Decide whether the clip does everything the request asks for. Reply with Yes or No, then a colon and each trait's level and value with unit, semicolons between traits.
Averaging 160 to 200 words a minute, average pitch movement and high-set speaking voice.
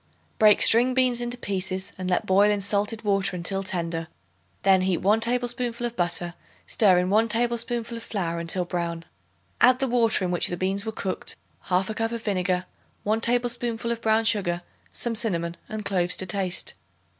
Yes: average, 180 wpm; average, 4.2 semitones; high, 205 Hz